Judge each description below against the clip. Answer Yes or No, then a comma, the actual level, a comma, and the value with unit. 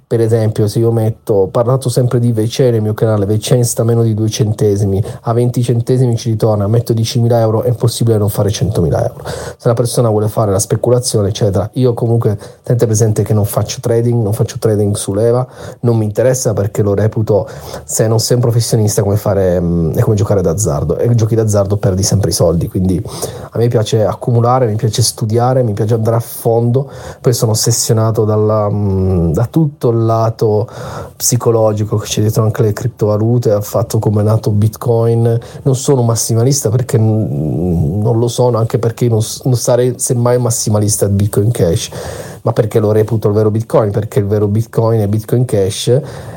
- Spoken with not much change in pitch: Yes, narrow, 2.3 semitones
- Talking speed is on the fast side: Yes, fast, 185 wpm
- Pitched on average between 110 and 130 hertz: Yes, low, 115 Hz